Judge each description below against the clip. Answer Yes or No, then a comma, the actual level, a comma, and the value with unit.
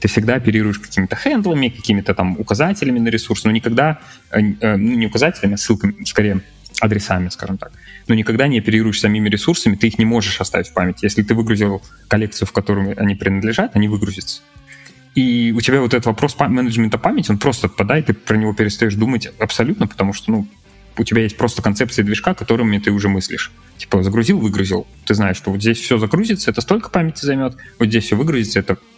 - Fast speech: Yes, fast, 195 wpm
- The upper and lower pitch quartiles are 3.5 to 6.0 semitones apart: No, narrow, 2.6 semitones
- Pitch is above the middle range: No, low, 110 Hz